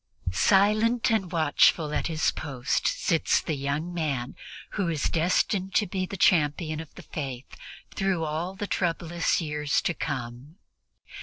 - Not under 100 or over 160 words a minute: Yes, average, 145 wpm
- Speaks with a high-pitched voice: No, medium, 165 Hz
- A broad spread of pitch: No, average, 3.9 semitones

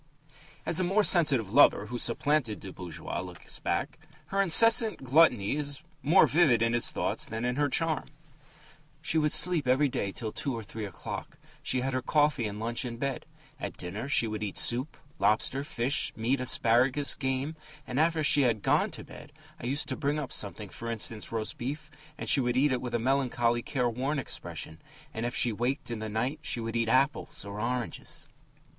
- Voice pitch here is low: Yes, low, 125 Hz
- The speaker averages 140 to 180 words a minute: No, average, 190 wpm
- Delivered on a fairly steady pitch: No, average, 4.2 semitones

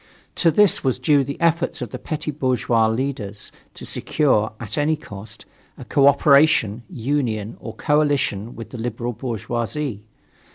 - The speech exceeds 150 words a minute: No, average, 140 wpm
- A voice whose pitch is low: Yes, low, 130 Hz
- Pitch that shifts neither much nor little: Yes, average, 4.7 semitones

